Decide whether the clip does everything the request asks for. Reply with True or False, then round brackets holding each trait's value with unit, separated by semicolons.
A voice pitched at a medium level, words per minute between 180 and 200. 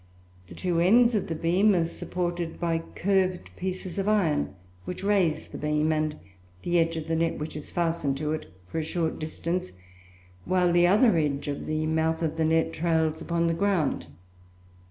True (165 Hz; 185 wpm)